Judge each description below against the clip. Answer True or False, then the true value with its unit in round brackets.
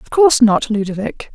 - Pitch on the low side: False (235 Hz)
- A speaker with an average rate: True (180 wpm)